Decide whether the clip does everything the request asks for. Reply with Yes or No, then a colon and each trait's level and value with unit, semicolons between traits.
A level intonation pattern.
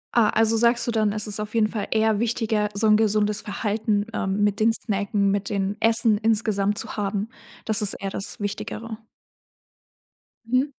Yes: narrow, 1.6 semitones